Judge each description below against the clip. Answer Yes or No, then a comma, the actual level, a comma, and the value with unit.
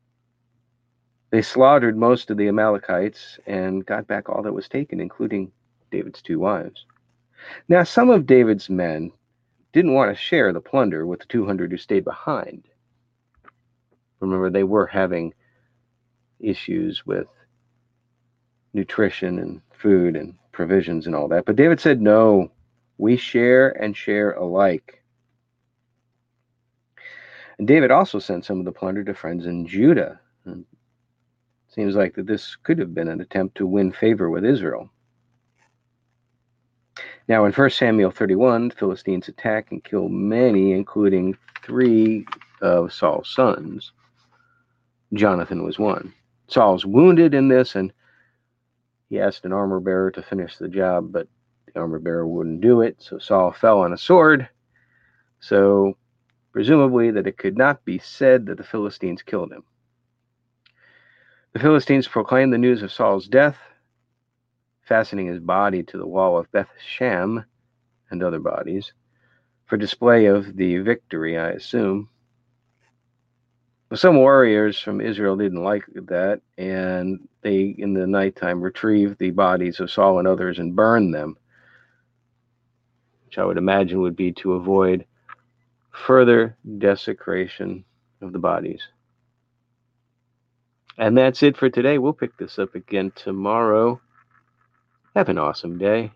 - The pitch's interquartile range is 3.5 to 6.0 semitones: Yes, average, 4.0 semitones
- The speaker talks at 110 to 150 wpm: Yes, slow, 135 wpm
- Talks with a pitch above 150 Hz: No, low, 120 Hz